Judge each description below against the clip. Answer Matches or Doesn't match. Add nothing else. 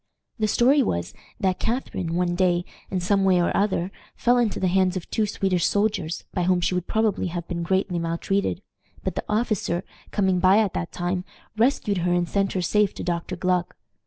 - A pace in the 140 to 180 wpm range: Doesn't match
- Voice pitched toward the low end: Doesn't match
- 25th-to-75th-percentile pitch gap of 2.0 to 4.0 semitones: Matches